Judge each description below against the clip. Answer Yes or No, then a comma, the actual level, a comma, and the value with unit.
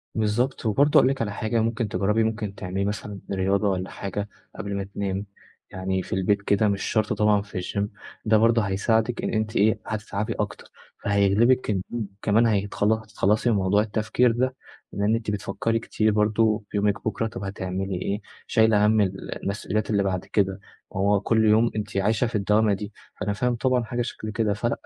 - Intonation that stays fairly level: Yes, narrow, 1.9 semitones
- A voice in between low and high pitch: No, low, 105 Hz